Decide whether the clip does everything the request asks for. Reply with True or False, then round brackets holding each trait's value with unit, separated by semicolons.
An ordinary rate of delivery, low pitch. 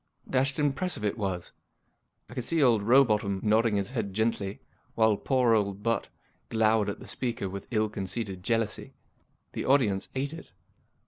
True (160 wpm; 110 Hz)